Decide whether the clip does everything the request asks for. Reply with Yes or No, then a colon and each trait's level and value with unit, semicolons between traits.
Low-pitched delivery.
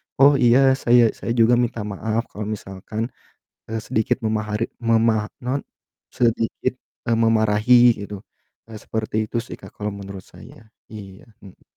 Yes: low, 110 Hz